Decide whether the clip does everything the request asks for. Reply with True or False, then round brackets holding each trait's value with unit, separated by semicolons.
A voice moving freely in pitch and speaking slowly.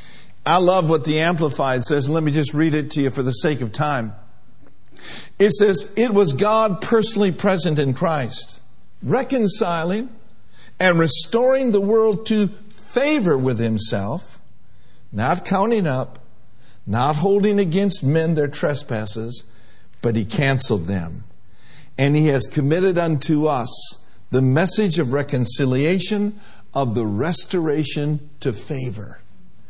True (7.2 semitones; 130 wpm)